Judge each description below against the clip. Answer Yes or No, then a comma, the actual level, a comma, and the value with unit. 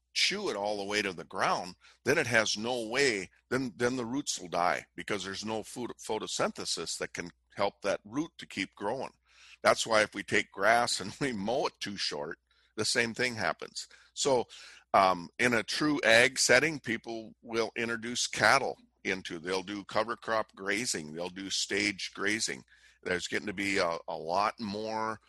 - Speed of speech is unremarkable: Yes, average, 185 wpm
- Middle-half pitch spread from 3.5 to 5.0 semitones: No, average, 2.8 semitones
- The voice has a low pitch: Yes, low, 110 Hz